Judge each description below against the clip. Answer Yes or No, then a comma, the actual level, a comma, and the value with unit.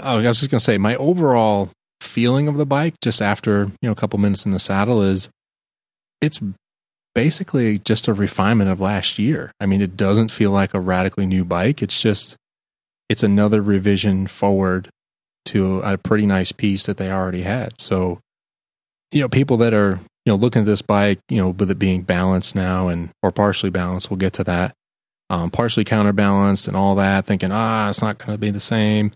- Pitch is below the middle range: Yes, low, 100 Hz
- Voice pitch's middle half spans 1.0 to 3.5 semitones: Yes, narrow, 2.5 semitones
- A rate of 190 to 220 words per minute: Yes, average, 200 wpm